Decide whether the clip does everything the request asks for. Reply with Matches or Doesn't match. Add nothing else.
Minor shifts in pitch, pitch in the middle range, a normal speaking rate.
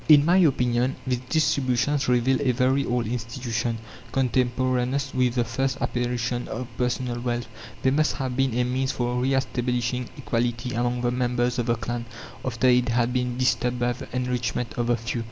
Doesn't match